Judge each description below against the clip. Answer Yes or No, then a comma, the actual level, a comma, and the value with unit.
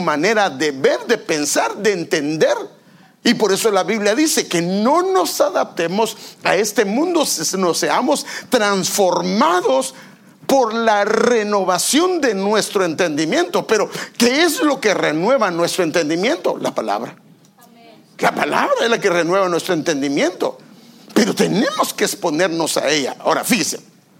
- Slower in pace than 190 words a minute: Yes, average, 140 wpm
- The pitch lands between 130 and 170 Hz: No, high, 215 Hz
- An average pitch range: No, wide, 5.8 semitones